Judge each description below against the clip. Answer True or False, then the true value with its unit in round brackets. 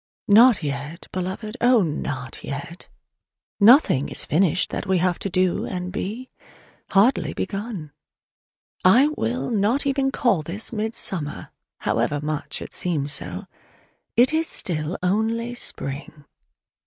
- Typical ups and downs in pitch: False (6.8 semitones)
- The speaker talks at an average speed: False (125 wpm)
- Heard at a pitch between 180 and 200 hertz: True (185 Hz)